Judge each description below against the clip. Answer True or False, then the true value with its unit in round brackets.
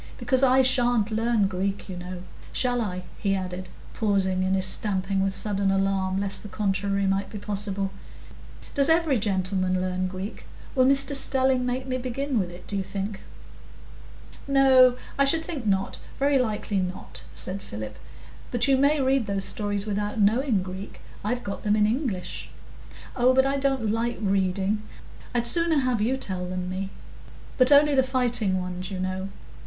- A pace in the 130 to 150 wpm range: False (170 wpm)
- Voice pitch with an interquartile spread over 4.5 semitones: True (5.0 semitones)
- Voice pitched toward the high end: True (205 Hz)